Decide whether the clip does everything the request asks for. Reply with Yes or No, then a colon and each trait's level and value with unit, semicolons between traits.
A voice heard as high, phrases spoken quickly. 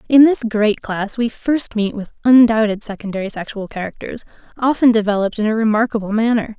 No: high, 220 Hz; average, 165 wpm